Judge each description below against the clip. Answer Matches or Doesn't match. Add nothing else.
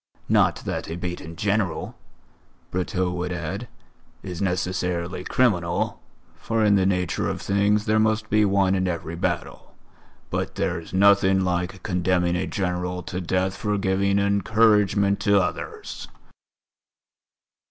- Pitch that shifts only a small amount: Matches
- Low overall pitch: Matches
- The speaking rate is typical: Doesn't match